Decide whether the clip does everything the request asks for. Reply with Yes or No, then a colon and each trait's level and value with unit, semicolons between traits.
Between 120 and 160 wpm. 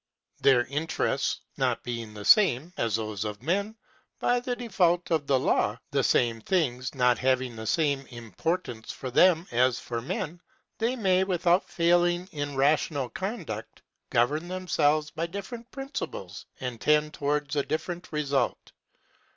Yes: average, 145 wpm